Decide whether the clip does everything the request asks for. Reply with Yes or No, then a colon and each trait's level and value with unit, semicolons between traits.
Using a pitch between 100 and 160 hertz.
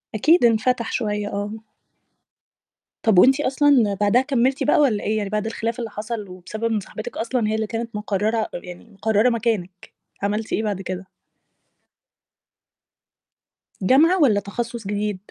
No: high, 220 Hz